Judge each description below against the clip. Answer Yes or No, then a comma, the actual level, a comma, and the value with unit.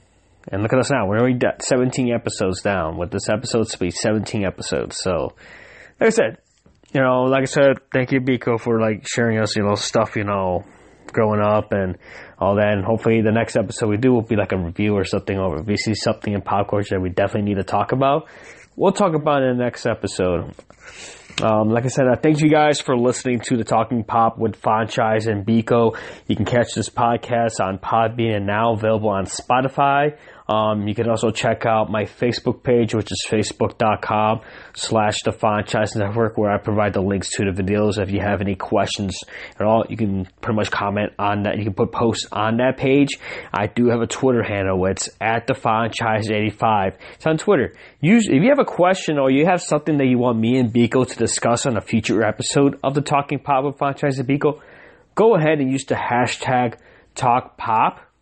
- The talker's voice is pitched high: No, low, 115 Hz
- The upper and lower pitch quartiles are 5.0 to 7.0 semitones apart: No, average, 3.7 semitones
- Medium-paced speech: No, fast, 210 wpm